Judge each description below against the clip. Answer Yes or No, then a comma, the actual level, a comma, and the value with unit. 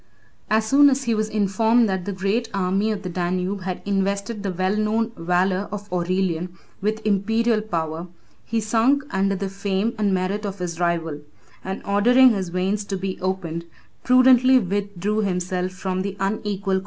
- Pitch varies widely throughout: No, average, 2.7 semitones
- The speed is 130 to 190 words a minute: Yes, average, 170 wpm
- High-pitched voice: Yes, high, 195 Hz